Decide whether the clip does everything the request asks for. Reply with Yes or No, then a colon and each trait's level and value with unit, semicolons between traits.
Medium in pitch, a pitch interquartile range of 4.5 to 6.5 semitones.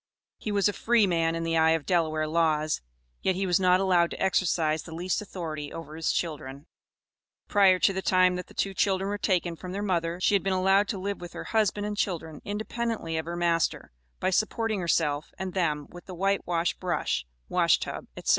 No: medium, 180 Hz; average, 3.0 semitones